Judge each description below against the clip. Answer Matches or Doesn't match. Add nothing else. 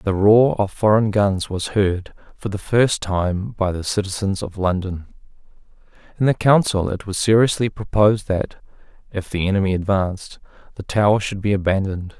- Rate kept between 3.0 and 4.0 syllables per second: Doesn't match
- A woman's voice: Doesn't match